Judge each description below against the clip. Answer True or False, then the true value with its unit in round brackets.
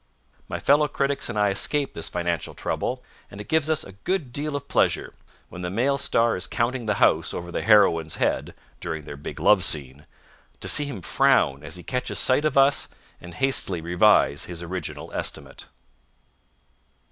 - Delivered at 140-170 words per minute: False (180 wpm)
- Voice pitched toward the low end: True (105 Hz)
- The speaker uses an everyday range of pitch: False (8.1 semitones)